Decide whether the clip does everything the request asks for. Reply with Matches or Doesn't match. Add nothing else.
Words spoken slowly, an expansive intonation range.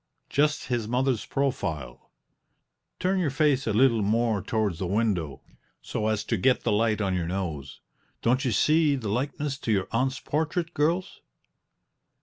Doesn't match